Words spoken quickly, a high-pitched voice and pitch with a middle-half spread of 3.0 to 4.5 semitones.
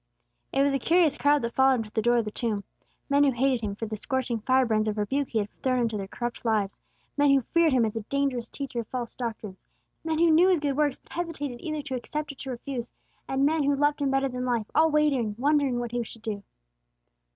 Yes: fast, 245 wpm; very high, 260 Hz; average, 3.8 semitones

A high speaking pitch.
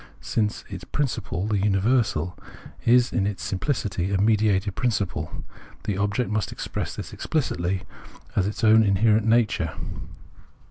No: low, 105 Hz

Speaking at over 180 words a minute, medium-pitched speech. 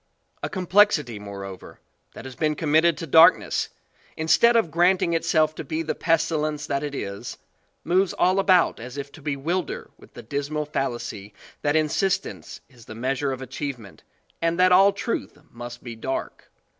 No: average, 170 wpm; medium, 150 Hz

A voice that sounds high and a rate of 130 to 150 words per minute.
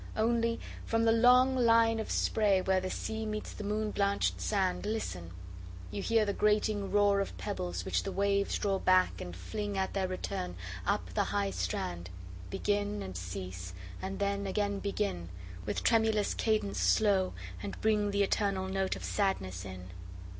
Yes: high, 200 Hz; average, 145 wpm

